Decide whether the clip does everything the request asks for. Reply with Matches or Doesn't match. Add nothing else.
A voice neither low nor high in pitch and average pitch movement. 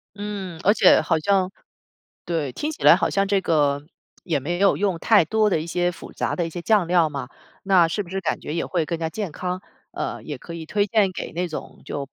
Matches